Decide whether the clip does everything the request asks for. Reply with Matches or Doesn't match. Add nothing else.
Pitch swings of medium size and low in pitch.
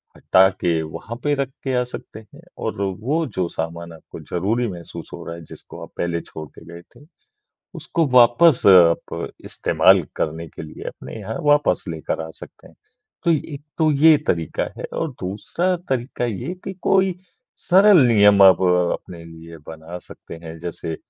Doesn't match